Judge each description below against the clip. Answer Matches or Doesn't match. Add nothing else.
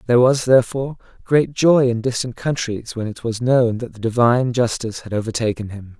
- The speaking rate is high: Doesn't match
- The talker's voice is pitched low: Matches